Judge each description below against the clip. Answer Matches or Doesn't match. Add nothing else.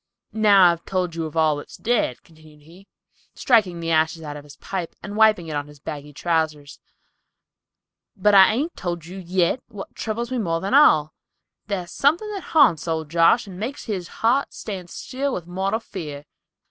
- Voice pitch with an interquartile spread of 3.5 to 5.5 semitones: Matches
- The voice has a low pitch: Doesn't match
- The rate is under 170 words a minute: Doesn't match